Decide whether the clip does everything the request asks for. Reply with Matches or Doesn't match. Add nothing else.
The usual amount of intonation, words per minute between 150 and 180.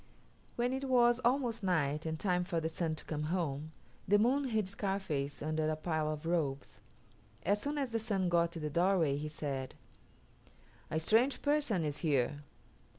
Doesn't match